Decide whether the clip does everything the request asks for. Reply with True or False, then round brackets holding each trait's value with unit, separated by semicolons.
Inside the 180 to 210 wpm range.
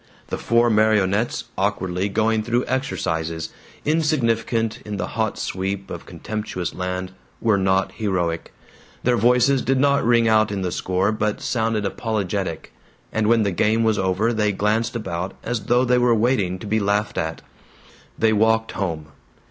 False (155 wpm)